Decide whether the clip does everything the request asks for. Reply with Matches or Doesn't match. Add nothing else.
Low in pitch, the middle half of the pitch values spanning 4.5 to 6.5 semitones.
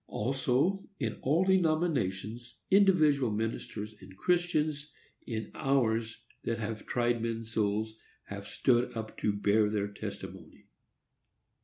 Matches